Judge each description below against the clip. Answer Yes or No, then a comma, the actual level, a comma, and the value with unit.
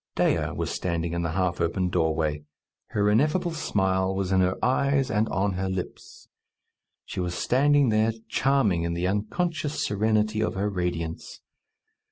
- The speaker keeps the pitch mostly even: No, average, 4.0 semitones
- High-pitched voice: No, very low, 95 Hz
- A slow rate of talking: No, average, 155 wpm